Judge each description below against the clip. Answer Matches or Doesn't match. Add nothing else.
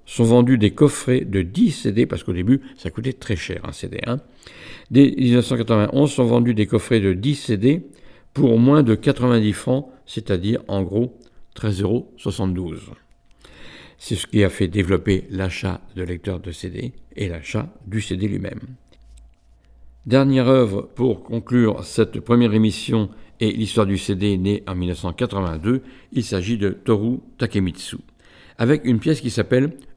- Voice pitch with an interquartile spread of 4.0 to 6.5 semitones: Matches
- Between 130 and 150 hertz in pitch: Doesn't match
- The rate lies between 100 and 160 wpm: Matches